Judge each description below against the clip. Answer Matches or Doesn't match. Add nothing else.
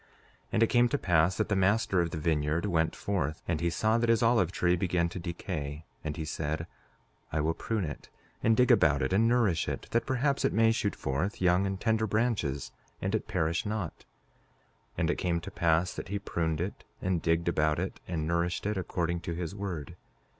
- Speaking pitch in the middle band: Doesn't match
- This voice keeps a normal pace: Doesn't match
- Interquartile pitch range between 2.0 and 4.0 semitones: Doesn't match